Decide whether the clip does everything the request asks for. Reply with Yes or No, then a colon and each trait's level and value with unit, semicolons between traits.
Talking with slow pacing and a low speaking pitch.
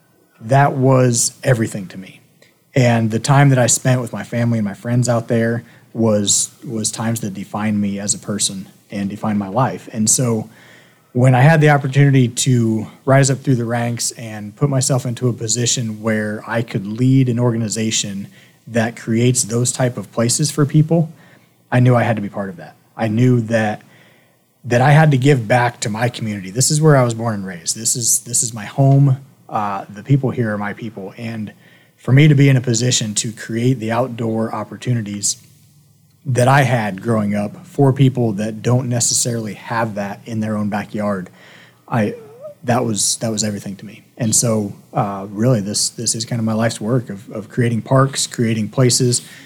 No: average, 195 wpm; low, 120 Hz